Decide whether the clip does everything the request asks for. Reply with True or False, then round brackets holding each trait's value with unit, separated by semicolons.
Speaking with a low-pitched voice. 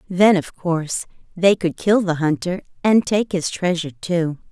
False (175 Hz)